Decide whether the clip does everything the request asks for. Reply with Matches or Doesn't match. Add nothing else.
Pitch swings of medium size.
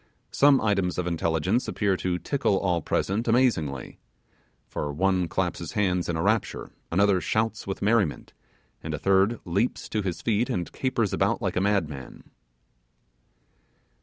Matches